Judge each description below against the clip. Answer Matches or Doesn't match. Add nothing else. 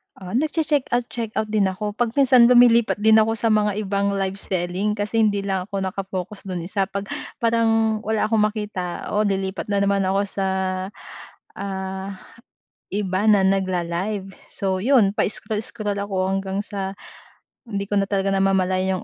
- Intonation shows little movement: Matches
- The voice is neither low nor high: Doesn't match